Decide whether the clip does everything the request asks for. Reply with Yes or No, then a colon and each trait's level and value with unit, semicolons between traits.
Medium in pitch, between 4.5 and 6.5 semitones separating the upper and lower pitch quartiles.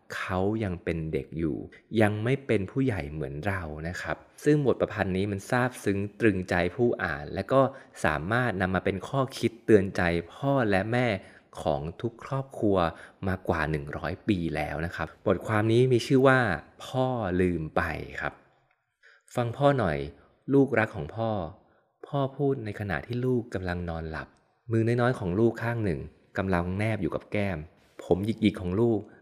No: low, 100 Hz; average, 5.3 semitones